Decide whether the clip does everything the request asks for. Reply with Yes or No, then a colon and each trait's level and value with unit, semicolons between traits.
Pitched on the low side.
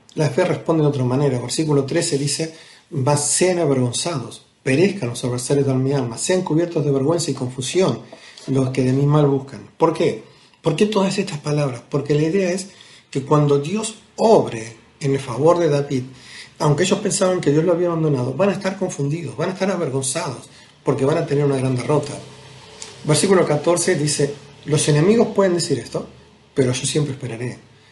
No: medium, 145 Hz